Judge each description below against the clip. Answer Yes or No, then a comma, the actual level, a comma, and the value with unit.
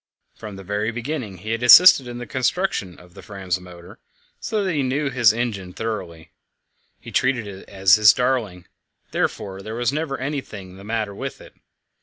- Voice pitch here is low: Yes, low, 110 Hz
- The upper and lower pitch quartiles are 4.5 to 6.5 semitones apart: Yes, average, 4.9 semitones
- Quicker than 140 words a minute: Yes, average, 180 wpm